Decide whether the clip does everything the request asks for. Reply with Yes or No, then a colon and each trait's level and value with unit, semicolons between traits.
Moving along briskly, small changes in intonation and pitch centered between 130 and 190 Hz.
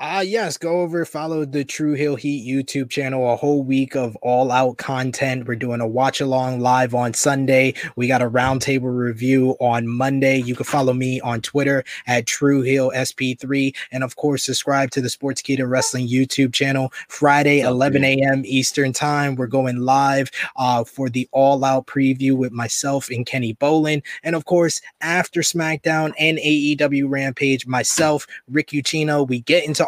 No: average, 175 wpm; narrow, 2.1 semitones; low, 135 Hz